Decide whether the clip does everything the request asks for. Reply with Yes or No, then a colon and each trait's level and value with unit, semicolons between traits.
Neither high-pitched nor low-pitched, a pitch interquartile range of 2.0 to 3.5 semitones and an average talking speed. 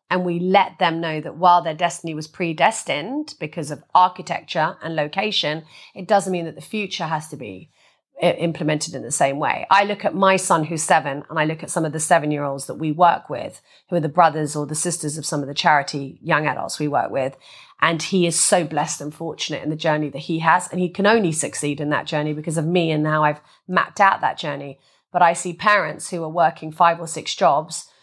No: medium, 165 Hz; average, 2.8 semitones; fast, 235 wpm